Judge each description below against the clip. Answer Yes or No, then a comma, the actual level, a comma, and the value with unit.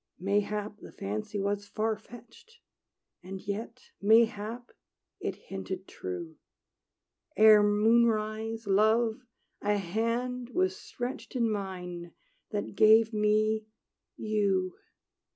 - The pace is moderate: No, slow, 100 wpm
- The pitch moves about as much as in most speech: No, narrow, 2.2 semitones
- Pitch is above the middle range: Yes, high, 215 Hz